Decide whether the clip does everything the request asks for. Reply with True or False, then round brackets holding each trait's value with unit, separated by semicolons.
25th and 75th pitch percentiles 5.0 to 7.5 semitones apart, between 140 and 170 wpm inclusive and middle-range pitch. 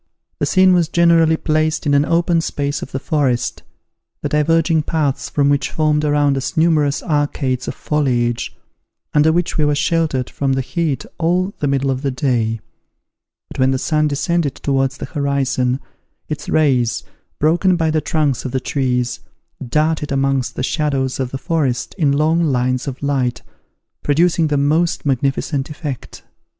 False (3.0 semitones; 160 wpm; 145 Hz)